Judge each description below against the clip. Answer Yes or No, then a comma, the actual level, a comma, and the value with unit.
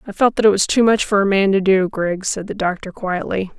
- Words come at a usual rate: No, fast, 285 wpm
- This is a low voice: No, high, 195 Hz